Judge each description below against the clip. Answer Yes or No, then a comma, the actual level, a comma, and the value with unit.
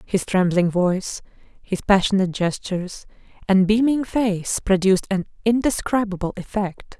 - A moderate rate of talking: No, slow, 110 wpm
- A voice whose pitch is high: Yes, high, 195 Hz